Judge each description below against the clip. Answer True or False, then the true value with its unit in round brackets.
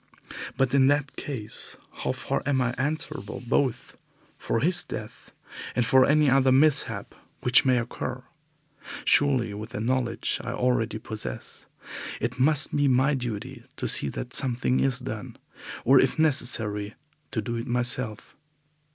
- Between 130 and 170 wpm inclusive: True (145 wpm)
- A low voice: True (125 Hz)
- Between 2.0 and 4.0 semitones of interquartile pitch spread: True (2.8 semitones)